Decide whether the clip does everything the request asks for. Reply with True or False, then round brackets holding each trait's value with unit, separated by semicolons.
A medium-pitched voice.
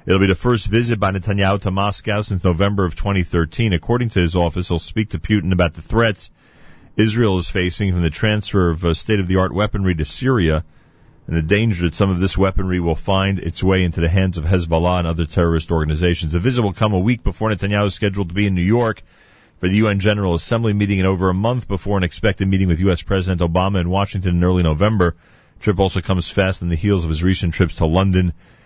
False (95 Hz)